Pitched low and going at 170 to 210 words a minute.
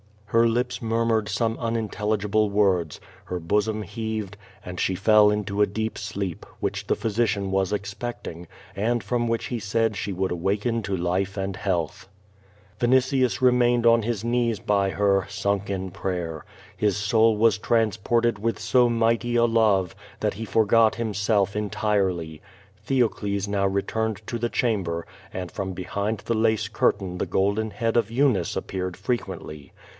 No: low, 105 Hz; average, 155 wpm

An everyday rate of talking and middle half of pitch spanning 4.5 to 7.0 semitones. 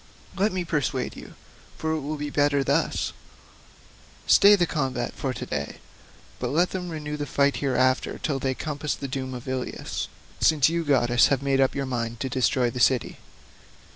No: average, 170 wpm; average, 2.8 semitones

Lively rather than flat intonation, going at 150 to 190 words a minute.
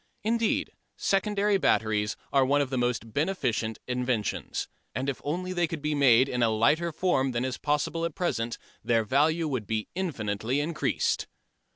Yes: wide, 6.2 semitones; average, 165 wpm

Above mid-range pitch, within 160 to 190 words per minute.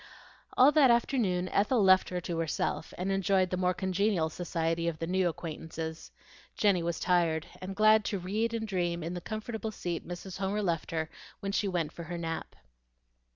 No: medium, 180 Hz; average, 185 wpm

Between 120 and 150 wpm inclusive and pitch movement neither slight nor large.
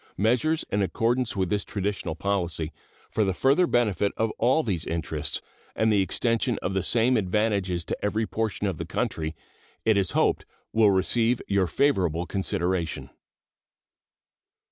Yes: average, 145 wpm; average, 3.7 semitones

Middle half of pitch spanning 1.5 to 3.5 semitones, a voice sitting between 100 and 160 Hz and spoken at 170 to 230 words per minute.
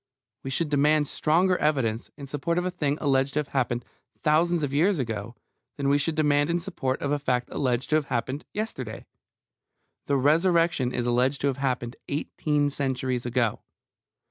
Yes: average, 3.2 semitones; medium, 140 Hz; average, 175 wpm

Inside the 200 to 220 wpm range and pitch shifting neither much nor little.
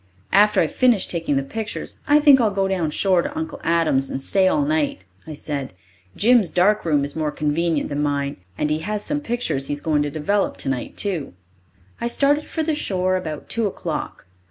No: fast, 205 wpm; wide, 7.1 semitones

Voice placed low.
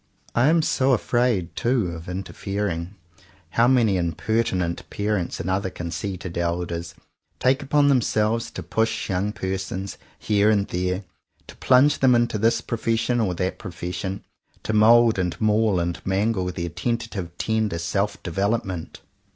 Yes: low, 100 Hz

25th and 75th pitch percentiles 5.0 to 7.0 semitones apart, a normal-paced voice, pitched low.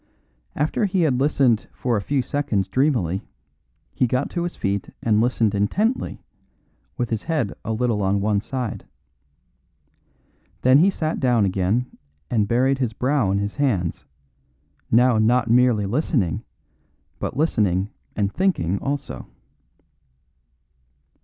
No: average, 5.3 semitones; slow, 130 wpm; low, 120 Hz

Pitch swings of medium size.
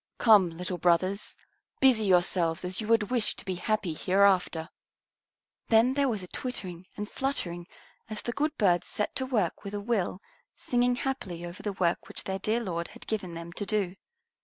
Yes: average, 4.2 semitones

